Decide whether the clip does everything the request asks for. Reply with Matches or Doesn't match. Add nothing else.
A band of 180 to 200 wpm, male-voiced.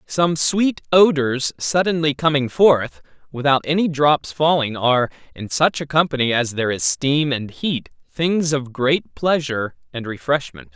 Doesn't match